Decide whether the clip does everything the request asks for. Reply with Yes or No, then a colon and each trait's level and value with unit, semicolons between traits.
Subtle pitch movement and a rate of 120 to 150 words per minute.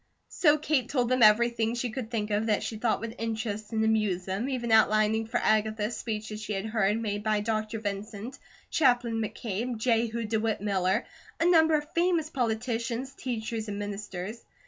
No: narrow, 2.2 semitones; average, 170 wpm